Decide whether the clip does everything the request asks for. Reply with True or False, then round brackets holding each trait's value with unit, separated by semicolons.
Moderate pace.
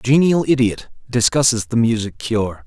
True (155 wpm)